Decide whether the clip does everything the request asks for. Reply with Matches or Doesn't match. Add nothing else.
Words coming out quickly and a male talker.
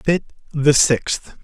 Doesn't match